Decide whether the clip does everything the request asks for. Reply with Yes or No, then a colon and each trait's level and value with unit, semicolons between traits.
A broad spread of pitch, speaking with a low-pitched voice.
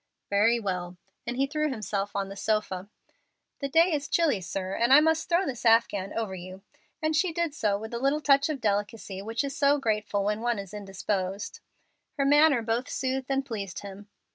No: wide, 5.7 semitones; high, 225 Hz